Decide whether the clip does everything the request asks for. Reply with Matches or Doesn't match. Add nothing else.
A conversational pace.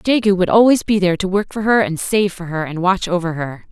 Doesn't match